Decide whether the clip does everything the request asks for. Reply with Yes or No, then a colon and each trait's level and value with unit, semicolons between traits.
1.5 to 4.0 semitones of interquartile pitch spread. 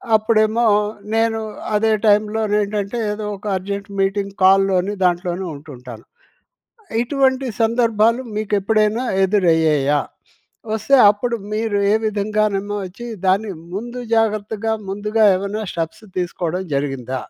Yes: average, 2.9 semitones